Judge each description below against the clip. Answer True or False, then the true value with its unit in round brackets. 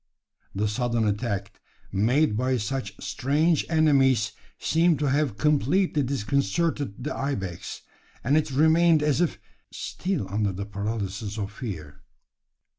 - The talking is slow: True (120 wpm)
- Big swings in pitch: True (6.6 semitones)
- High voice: False (130 Hz)